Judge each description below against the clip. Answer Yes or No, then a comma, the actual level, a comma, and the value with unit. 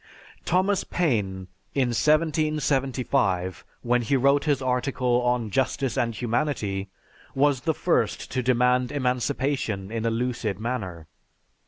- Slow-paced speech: Yes, slow, 120 wpm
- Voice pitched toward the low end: Yes, low, 125 Hz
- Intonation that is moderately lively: Yes, average, 3.5 semitones